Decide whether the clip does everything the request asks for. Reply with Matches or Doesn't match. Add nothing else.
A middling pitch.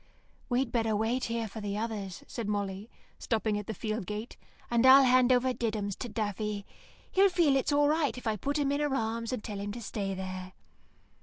Doesn't match